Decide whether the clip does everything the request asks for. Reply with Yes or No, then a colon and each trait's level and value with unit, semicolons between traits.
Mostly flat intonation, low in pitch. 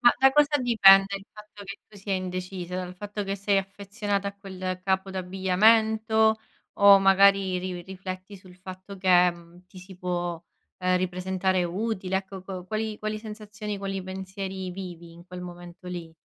No: narrow, 1.7 semitones; high, 190 Hz